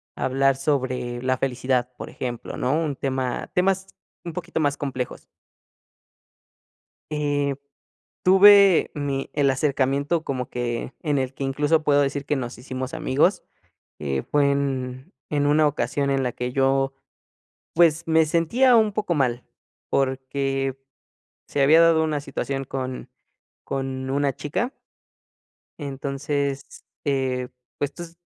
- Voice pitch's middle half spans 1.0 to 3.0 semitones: Yes, narrow, 2.5 semitones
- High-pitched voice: No, medium, 140 Hz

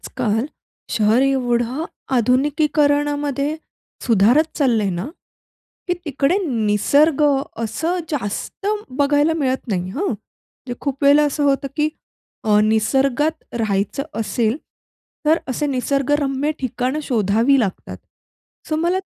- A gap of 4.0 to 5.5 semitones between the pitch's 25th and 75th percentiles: Yes, average, 4.5 semitones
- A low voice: No, very high, 270 Hz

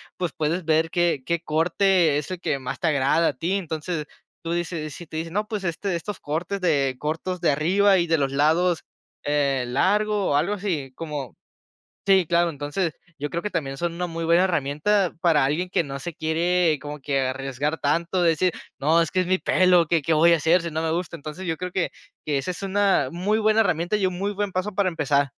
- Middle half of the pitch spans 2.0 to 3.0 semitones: No, average, 3.6 semitones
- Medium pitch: Yes, medium, 165 Hz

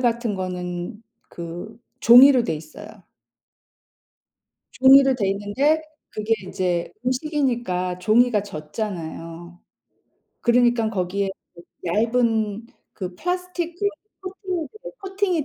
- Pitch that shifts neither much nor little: No, wide, 6.0 semitones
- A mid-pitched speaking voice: No, high, 220 Hz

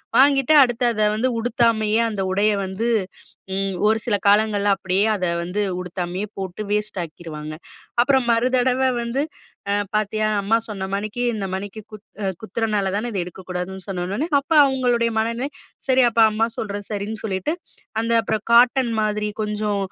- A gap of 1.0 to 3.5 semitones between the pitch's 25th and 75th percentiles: Yes, average, 3.1 semitones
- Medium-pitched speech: No, high, 215 Hz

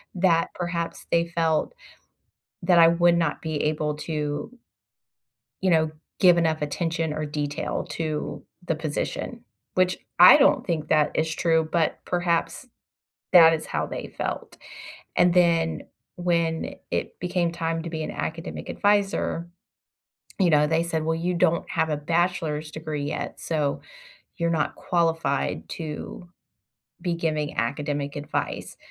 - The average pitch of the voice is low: No, medium, 165 Hz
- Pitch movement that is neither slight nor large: No, narrow, 1.9 semitones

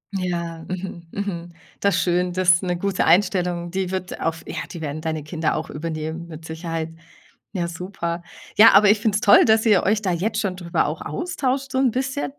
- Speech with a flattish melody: No, average, 3.3 semitones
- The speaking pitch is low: No, medium, 180 Hz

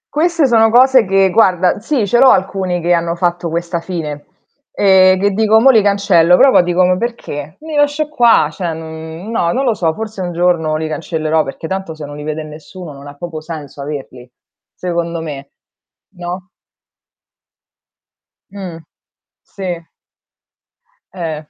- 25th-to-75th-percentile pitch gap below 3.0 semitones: No, average, 4.2 semitones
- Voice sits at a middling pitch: Yes, medium, 175 Hz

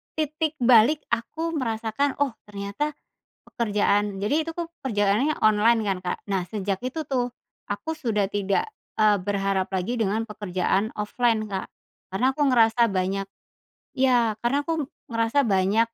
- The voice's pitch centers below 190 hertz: No, high, 225 Hz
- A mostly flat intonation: No, average, 4.7 semitones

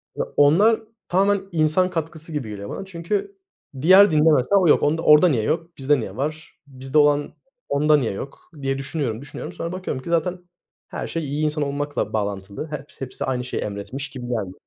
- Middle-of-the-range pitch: Yes, medium, 150 Hz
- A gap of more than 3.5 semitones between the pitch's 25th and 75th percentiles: Yes, average, 4.0 semitones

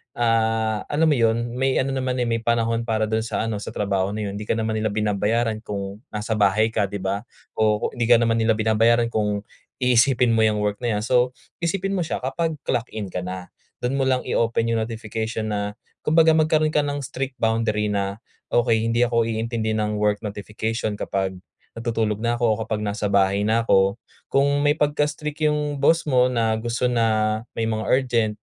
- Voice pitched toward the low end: Yes, low, 115 Hz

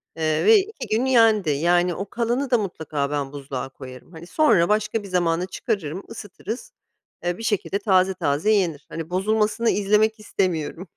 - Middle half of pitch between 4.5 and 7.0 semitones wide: Yes, average, 5.1 semitones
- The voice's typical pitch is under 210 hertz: Yes, high, 190 Hz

